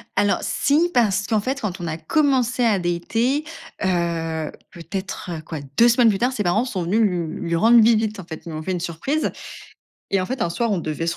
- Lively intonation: Yes, wide, 5.7 semitones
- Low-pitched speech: No, high, 195 Hz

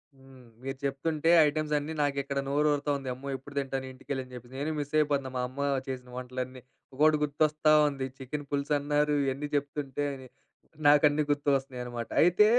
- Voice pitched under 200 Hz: Yes, medium, 140 Hz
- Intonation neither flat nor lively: No, narrow, 1.9 semitones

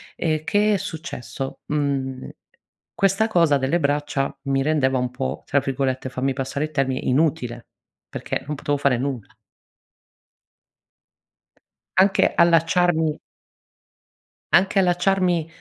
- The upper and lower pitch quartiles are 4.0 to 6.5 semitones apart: Yes, average, 4.3 semitones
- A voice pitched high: No, medium, 145 Hz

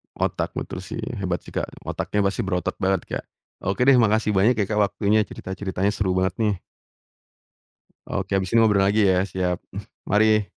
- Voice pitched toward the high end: No, low, 100 Hz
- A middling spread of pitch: No, narrow, 2.3 semitones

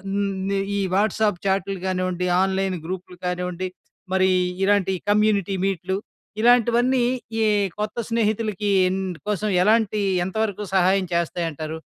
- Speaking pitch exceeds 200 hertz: No, high, 195 Hz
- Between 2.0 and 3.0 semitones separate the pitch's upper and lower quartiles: Yes, narrow, 2.4 semitones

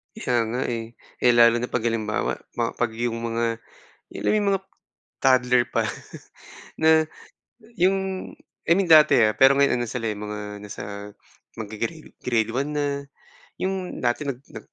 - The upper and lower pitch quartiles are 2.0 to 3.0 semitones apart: No, average, 4.6 semitones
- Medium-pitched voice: No, low, 120 Hz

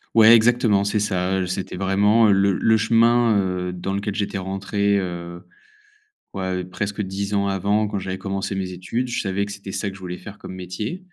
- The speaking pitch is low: Yes, low, 100 Hz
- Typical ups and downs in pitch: No, narrow, 2.0 semitones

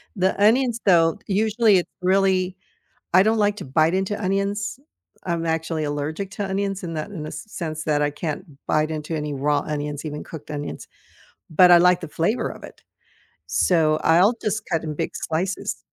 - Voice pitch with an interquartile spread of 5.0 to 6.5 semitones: No, average, 4.3 semitones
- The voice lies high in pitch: No, medium, 170 Hz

